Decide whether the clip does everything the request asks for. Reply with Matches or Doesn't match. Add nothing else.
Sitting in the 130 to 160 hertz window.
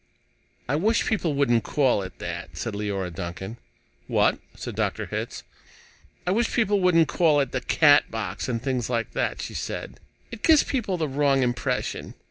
Matches